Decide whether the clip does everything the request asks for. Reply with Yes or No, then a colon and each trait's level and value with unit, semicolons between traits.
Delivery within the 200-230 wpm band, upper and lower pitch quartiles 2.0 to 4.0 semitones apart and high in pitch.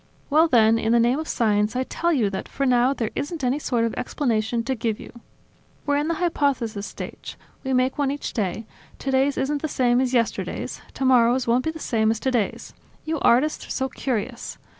Yes: fast, 205 wpm; average, 3.5 semitones; very high, 255 Hz